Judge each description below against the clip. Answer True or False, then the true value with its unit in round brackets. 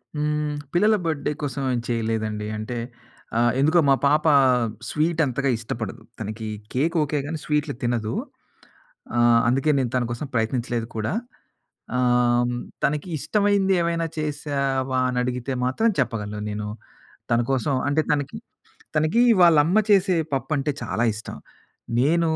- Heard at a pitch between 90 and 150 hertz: True (135 Hz)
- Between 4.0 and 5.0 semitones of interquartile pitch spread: True (4.3 semitones)